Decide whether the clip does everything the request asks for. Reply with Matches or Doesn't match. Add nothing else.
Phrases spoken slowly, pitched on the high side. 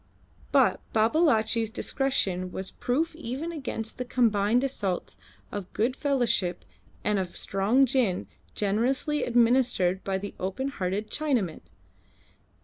Matches